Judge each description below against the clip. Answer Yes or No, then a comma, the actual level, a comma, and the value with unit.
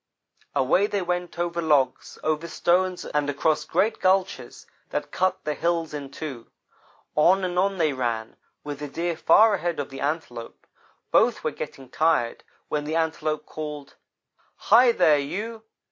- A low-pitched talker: No, medium, 160 Hz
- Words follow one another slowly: No, average, 155 wpm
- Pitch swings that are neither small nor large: Yes, average, 3.6 semitones